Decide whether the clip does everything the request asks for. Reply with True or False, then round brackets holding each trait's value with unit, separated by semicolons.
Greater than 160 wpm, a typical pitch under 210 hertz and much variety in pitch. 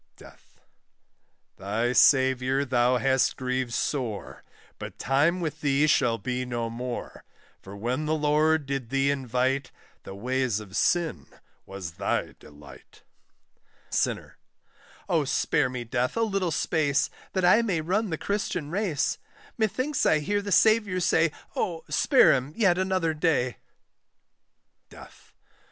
False (135 wpm; 140 Hz; 5.7 semitones)